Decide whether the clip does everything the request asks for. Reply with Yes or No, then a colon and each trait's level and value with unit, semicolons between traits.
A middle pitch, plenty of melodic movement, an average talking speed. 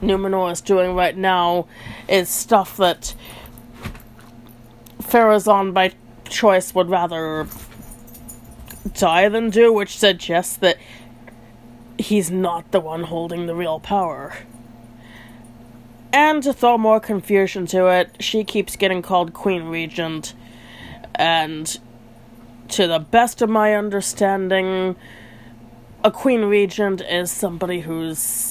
No: medium, 175 Hz; wide, 8.8 semitones; slow, 110 wpm